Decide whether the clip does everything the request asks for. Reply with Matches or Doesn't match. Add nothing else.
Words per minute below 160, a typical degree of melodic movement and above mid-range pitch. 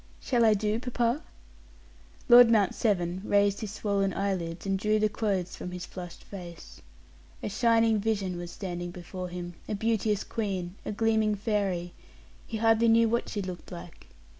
Doesn't match